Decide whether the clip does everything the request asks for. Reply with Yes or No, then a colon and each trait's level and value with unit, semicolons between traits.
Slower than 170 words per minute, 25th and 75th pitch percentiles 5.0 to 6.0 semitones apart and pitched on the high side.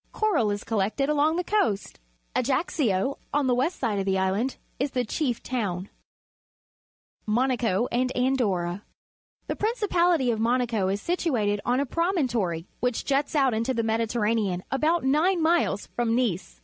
Yes: average, 150 wpm; wide, 5.6 semitones; high, 245 Hz